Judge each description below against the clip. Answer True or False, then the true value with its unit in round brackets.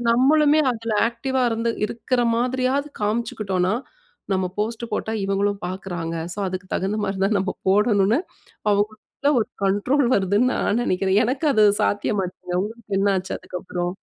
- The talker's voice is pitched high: True (210 Hz)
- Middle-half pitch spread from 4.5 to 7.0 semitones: False (3.5 semitones)